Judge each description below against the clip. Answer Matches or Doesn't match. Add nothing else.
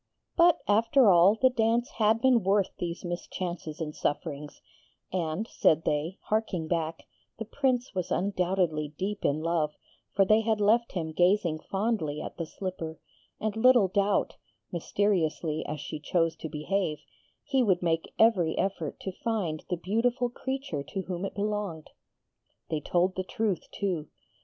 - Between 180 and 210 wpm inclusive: Doesn't match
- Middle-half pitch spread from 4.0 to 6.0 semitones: Matches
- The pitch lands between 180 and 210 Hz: Matches